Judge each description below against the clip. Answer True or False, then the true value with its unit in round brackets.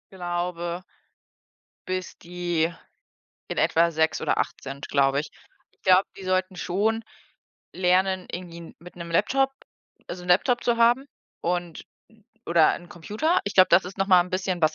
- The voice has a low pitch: False (180 Hz)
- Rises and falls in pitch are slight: True (2.0 semitones)